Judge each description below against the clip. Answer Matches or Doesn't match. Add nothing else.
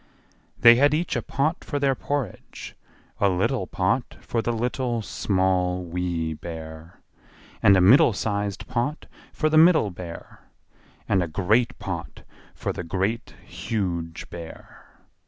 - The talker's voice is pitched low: Matches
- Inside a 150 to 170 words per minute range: Doesn't match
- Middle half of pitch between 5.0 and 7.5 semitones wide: Matches